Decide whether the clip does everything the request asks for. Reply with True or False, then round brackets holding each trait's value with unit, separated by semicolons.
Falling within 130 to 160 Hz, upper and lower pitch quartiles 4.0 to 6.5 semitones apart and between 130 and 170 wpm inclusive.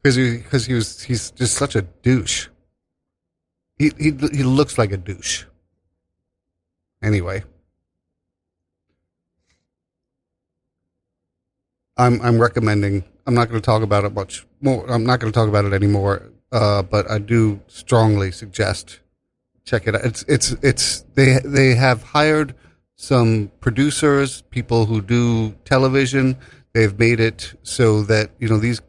False (110 Hz; 4.7 semitones; 140 wpm)